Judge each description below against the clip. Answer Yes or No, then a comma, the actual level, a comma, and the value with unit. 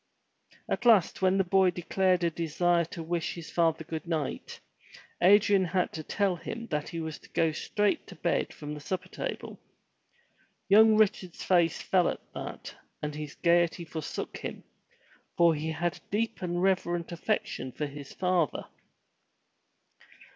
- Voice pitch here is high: No, medium, 175 Hz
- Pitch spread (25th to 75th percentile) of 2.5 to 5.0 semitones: Yes, average, 2.8 semitones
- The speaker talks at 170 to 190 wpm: No, average, 155 wpm